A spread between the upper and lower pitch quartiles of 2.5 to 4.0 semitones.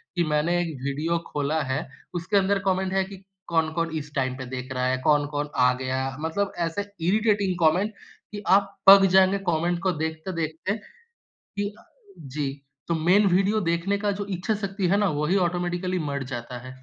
No: average, 4.7 semitones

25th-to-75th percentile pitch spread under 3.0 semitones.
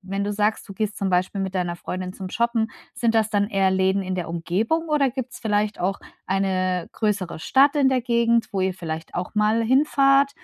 No: average, 4.0 semitones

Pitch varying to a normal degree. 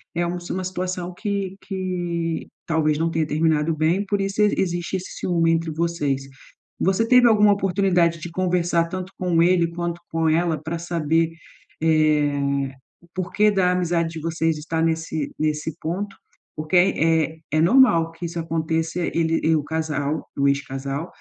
No: narrow, 2.1 semitones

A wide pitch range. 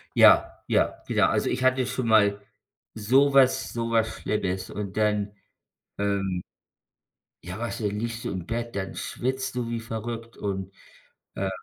No: average, 2.8 semitones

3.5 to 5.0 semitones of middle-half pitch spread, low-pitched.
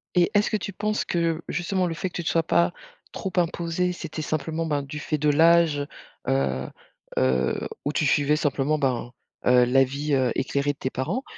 No: average, 4.0 semitones; medium, 150 Hz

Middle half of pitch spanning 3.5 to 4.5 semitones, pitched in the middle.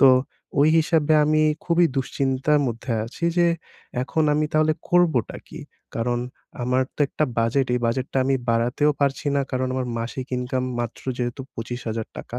No: average, 3.8 semitones; low, 130 Hz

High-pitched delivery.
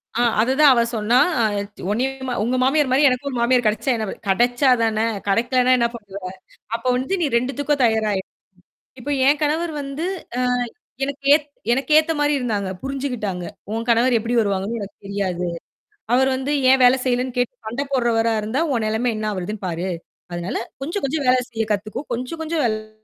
Yes: high, 245 Hz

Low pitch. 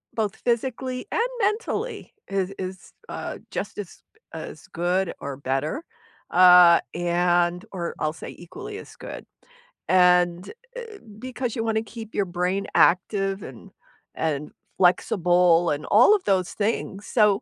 No: medium, 185 Hz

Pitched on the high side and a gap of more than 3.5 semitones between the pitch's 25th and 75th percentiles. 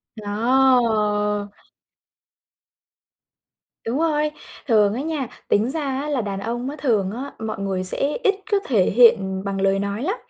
Yes: high, 225 Hz; average, 4.9 semitones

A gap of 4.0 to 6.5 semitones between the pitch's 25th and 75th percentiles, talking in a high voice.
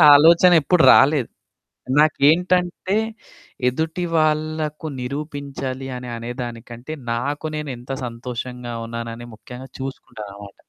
No: average, 4.4 semitones; low, 135 Hz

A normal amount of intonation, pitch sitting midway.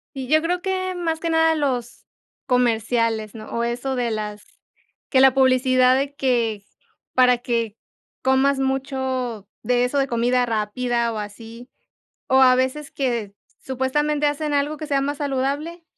No: average, 3.2 semitones; very high, 260 Hz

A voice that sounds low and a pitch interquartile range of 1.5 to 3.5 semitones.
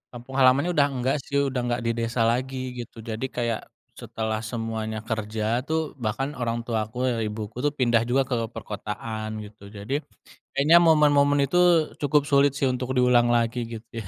Yes: low, 120 Hz; average, 3.2 semitones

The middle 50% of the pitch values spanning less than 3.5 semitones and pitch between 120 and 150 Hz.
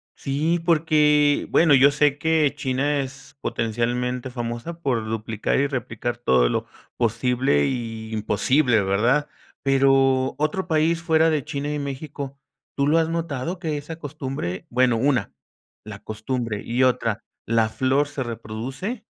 No: average, 4.2 semitones; low, 135 Hz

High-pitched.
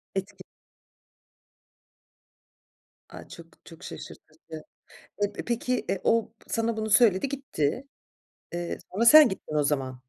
Yes: high, 210 Hz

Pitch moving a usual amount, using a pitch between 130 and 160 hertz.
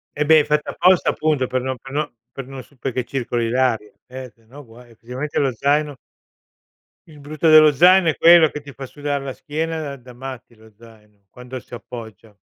Yes: average, 3.7 semitones; low, 135 Hz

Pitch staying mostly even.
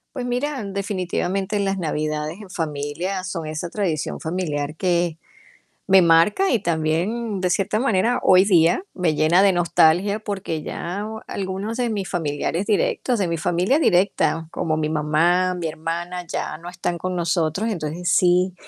No: average, 3.3 semitones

